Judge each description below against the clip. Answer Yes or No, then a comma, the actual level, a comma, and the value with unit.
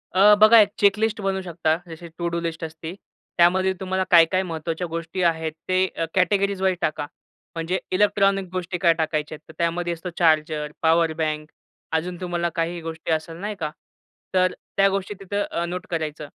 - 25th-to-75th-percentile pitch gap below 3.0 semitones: Yes, narrow, 2.6 semitones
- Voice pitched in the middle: Yes, medium, 170 Hz